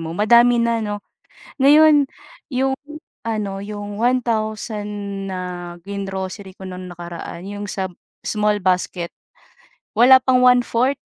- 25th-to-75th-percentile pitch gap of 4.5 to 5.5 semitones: No, average, 4.0 semitones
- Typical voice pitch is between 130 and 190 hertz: No, high, 210 Hz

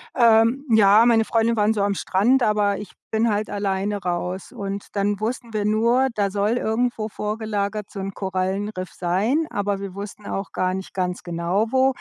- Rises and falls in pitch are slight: Yes, narrow, 2.3 semitones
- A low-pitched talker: No, high, 205 Hz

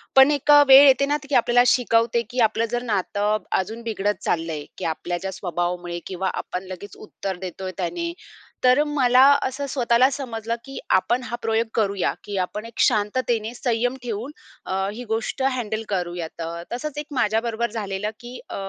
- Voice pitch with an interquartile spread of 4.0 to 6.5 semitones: Yes, average, 4.6 semitones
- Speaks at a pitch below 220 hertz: No, high, 225 Hz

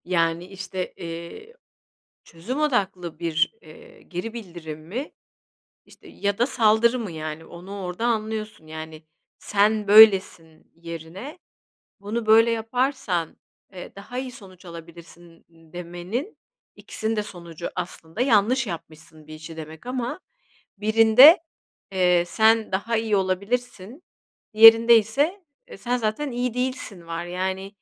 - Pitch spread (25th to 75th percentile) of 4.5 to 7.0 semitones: Yes, average, 5.2 semitones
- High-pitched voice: Yes, high, 200 Hz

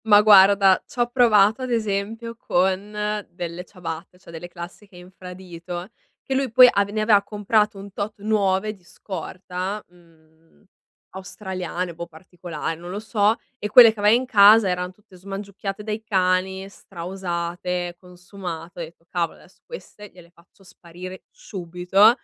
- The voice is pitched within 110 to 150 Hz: No, high, 190 Hz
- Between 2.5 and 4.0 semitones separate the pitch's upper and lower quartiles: Yes, average, 2.8 semitones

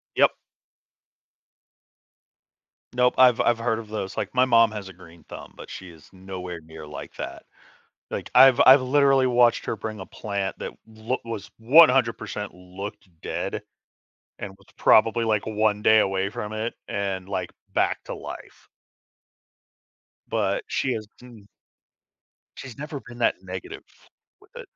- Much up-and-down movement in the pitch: No, average, 4.0 semitones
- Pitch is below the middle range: Yes, low, 110 Hz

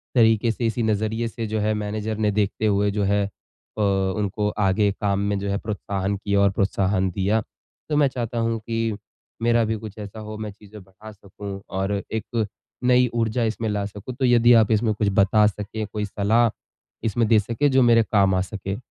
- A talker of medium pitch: No, low, 105 Hz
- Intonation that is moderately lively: No, narrow, 2.1 semitones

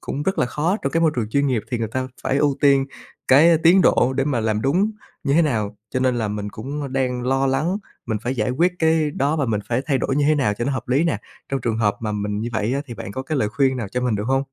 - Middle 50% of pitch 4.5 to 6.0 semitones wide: No, average, 4.1 semitones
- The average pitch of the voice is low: Yes, low, 130 Hz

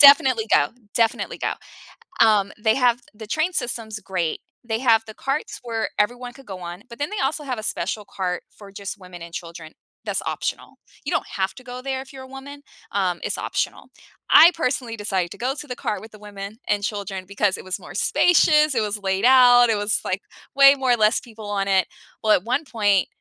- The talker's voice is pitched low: No, high, 220 Hz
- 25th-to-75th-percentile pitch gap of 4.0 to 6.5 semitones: Yes, average, 4.6 semitones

